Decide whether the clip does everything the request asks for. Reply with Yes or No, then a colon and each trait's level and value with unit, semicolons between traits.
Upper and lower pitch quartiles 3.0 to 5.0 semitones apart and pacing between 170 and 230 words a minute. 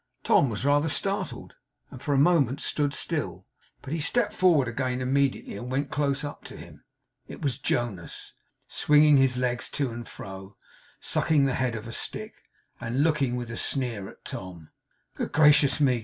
Yes: average, 3.4 semitones; average, 175 wpm